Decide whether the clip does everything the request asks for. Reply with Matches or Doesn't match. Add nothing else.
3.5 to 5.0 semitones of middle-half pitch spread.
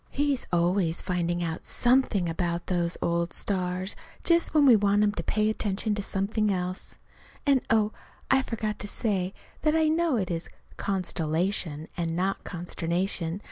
Matches